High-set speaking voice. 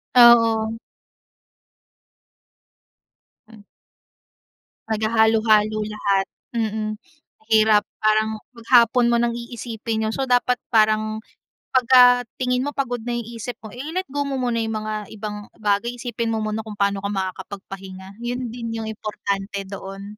Yes: high, 220 Hz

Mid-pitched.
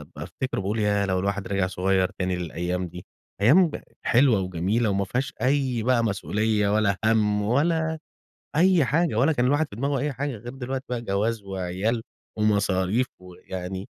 No: low, 105 Hz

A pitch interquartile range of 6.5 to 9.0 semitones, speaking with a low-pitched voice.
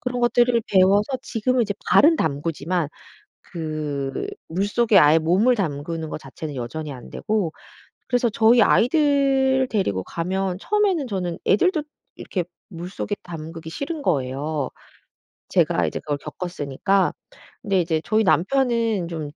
No: wide, 7.2 semitones; medium, 185 Hz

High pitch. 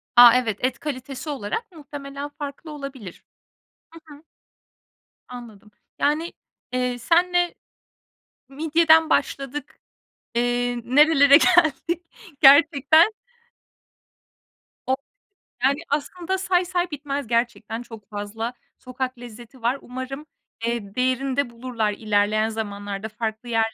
Yes: very high, 260 Hz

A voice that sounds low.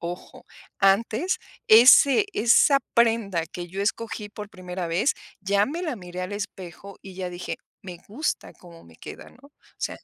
No: high, 200 Hz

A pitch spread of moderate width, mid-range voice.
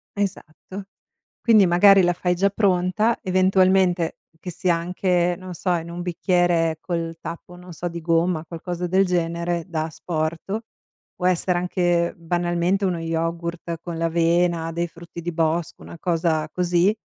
No: narrow, 1.6 semitones; medium, 175 Hz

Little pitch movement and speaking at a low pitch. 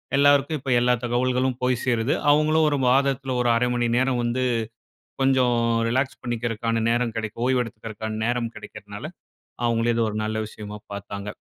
Yes: narrow, 2.3 semitones; low, 120 Hz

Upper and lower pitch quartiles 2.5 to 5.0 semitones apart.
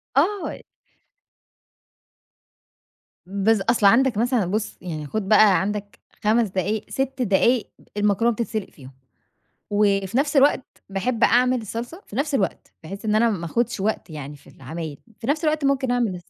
Yes: average, 4.2 semitones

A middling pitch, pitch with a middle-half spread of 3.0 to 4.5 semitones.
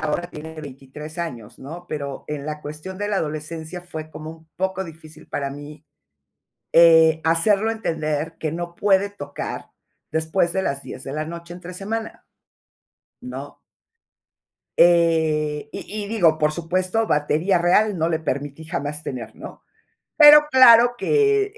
Yes: medium, 165 Hz; average, 3.8 semitones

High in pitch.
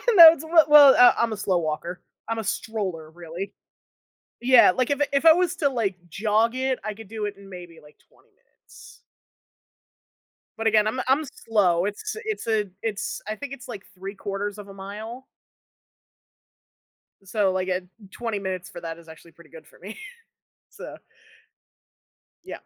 Yes: high, 210 Hz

